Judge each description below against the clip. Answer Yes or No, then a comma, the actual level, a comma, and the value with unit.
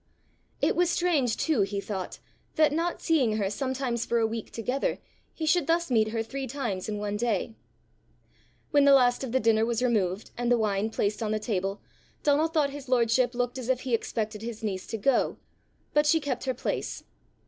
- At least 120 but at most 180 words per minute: No, average, 200 wpm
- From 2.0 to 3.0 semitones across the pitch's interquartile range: No, average, 4.2 semitones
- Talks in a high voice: Yes, high, 240 Hz